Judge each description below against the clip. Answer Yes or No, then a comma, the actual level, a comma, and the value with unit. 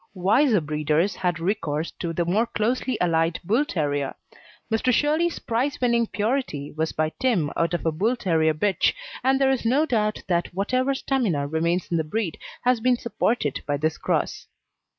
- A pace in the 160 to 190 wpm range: Yes, average, 170 wpm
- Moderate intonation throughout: No, wide, 7.4 semitones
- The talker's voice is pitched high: Yes, high, 195 Hz